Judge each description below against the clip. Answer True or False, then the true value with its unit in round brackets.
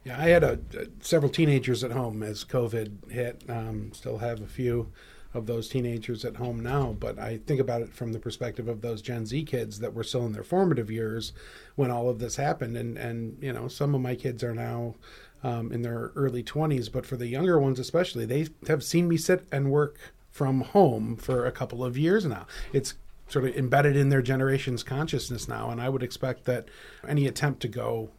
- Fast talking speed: True (215 wpm)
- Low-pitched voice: True (125 Hz)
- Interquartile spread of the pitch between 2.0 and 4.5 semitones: True (2.9 semitones)